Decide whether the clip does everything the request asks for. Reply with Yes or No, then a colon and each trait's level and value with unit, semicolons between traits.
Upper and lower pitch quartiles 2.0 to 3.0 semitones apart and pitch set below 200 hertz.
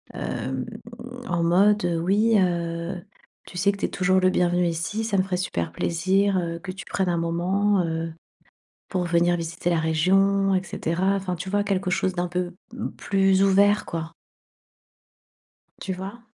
Yes: narrow, 2.4 semitones; medium, 185 Hz